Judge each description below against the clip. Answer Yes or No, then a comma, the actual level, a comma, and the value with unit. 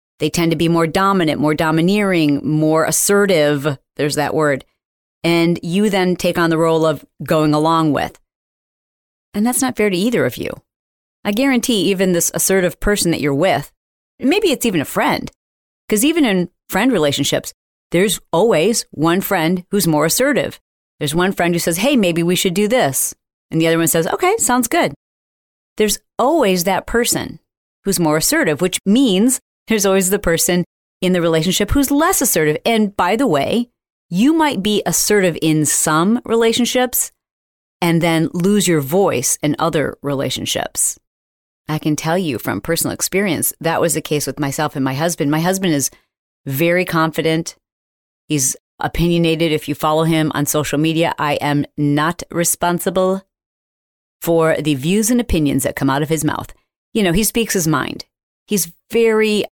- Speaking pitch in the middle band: Yes, medium, 170 Hz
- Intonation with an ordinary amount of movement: Yes, average, 4.7 semitones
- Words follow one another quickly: No, average, 170 wpm